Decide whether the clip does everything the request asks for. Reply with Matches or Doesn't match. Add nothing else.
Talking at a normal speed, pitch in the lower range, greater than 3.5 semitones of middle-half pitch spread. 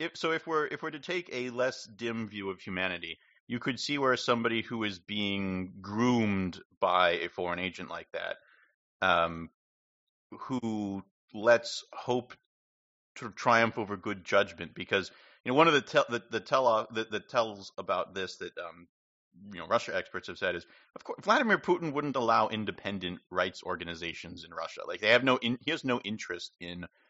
Matches